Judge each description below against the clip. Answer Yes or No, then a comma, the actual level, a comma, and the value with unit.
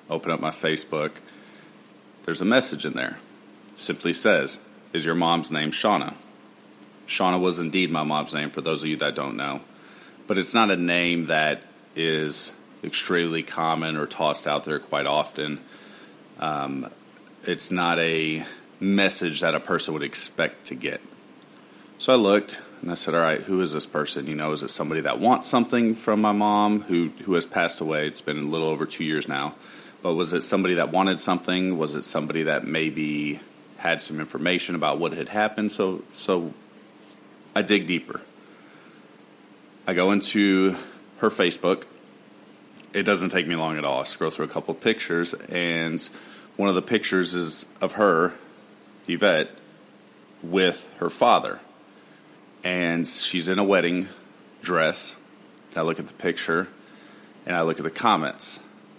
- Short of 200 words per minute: Yes, average, 170 wpm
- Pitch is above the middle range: No, very low, 90 Hz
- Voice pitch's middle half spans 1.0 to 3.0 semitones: No, average, 3.8 semitones